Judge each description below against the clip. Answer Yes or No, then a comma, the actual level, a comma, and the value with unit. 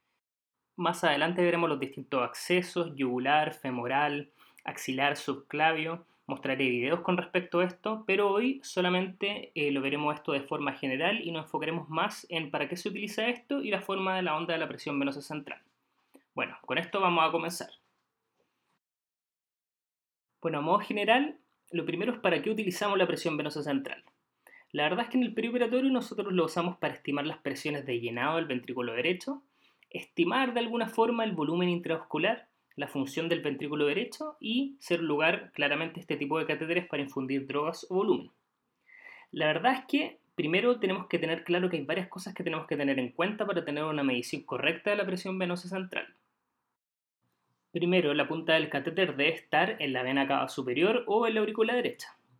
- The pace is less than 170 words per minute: No, average, 180 wpm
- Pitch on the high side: No, medium, 170 Hz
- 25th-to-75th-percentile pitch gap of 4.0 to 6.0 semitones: Yes, wide, 5.4 semitones